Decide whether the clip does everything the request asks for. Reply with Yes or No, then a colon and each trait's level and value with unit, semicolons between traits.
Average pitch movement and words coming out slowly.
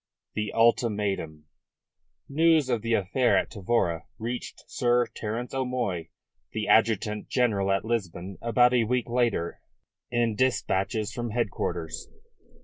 Yes: average, 3.7 semitones; slow, 120 wpm